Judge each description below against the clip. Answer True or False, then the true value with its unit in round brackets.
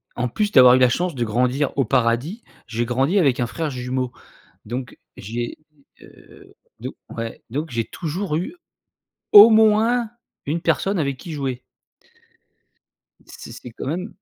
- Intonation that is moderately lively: False (6.5 semitones)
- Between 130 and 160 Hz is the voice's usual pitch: True (135 Hz)